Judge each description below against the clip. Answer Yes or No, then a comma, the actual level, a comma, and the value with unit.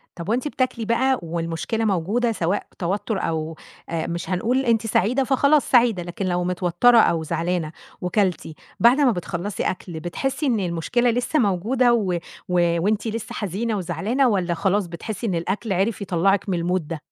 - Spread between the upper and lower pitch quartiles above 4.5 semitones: Yes, average, 5.1 semitones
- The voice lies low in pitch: No, high, 195 Hz